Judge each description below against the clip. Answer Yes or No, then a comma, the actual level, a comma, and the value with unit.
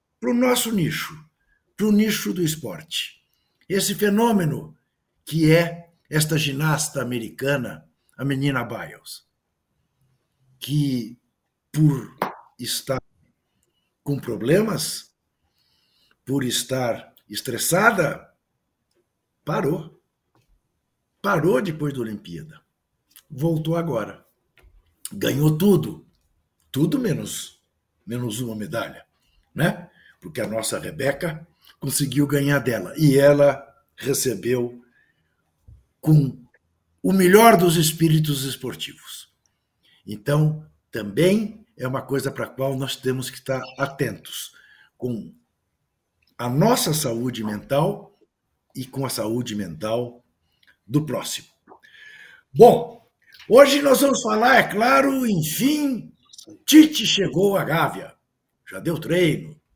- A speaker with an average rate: No, slow, 100 wpm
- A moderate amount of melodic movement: No, wide, 6.1 semitones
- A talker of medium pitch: Yes, medium, 145 Hz